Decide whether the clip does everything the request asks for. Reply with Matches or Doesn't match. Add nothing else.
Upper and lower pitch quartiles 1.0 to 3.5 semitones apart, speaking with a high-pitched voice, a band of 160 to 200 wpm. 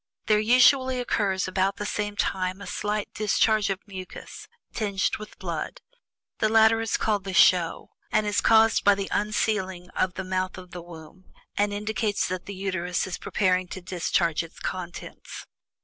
Matches